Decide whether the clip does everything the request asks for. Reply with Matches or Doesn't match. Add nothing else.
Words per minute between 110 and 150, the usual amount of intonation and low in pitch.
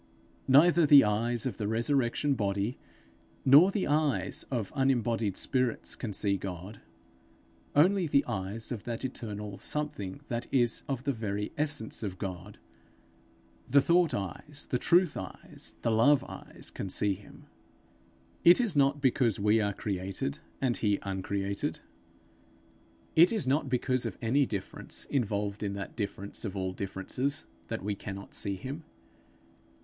Doesn't match